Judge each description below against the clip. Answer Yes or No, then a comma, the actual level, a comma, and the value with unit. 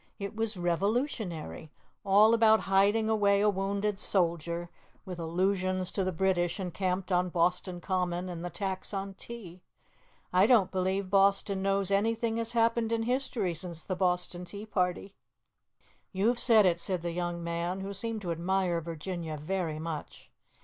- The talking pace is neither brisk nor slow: Yes, average, 155 wpm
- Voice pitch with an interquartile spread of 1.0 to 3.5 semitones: Yes, narrow, 2.6 semitones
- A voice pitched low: No, high, 190 Hz